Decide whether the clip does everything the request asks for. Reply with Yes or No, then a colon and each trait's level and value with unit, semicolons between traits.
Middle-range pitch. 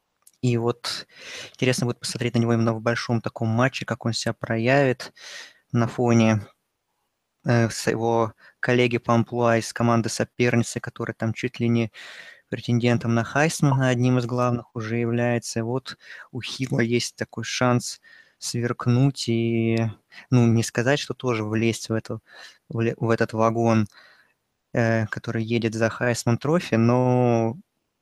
No: low, 120 Hz